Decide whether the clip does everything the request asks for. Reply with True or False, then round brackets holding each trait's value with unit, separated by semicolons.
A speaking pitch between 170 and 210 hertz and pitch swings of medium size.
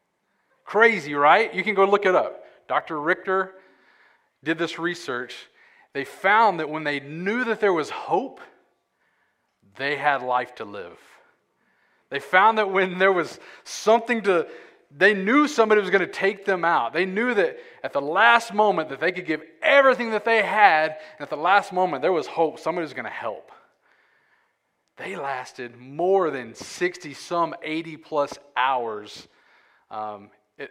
False (185 Hz; 5.8 semitones)